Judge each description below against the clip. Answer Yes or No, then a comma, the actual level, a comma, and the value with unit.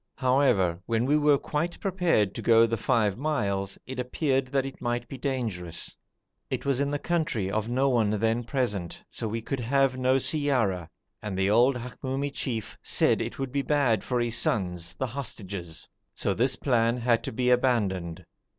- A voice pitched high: No, low, 120 Hz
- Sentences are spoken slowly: No, average, 180 wpm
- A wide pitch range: No, average, 4.3 semitones